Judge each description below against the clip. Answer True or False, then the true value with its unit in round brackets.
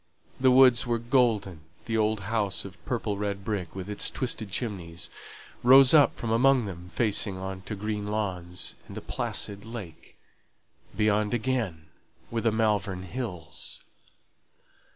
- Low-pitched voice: True (105 Hz)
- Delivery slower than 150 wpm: True (140 wpm)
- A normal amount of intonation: True (3.6 semitones)